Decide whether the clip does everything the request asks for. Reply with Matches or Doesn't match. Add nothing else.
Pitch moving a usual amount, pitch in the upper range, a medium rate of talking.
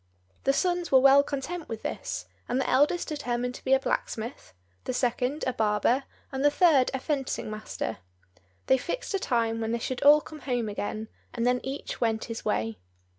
Matches